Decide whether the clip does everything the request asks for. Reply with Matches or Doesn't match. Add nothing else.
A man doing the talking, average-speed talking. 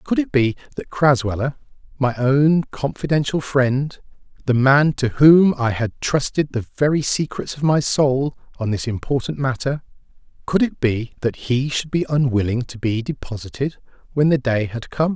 Matches